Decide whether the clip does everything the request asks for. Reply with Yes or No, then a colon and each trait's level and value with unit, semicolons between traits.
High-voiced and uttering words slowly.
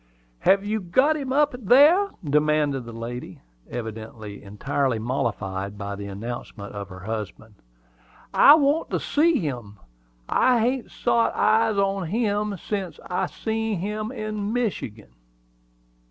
No: medium, 175 Hz; slow, 130 wpm